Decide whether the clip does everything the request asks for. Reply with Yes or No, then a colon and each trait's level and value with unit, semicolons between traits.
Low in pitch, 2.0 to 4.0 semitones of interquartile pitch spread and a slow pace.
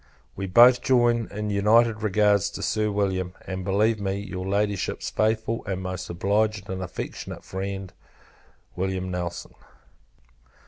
Yes: low, 100 Hz; narrow, 2.5 semitones; slow, 130 wpm